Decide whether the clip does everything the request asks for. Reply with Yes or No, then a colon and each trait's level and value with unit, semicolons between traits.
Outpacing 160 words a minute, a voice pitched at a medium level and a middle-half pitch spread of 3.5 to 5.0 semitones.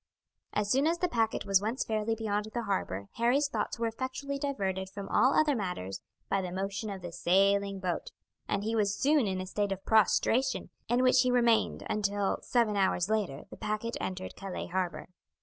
No: average, 190 wpm; high, 210 Hz; average, 3.8 semitones